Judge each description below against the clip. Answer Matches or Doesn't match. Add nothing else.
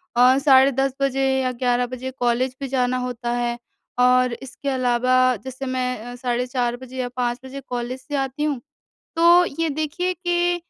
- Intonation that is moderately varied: Doesn't match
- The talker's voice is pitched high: Matches